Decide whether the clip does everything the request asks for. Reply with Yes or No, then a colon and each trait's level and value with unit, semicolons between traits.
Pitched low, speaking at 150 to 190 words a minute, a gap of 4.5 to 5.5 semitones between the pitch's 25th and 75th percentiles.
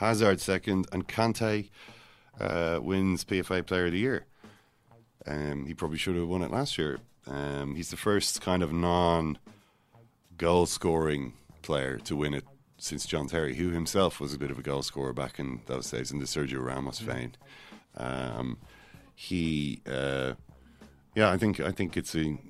Yes: very low, 85 Hz; average, 170 wpm; average, 4.8 semitones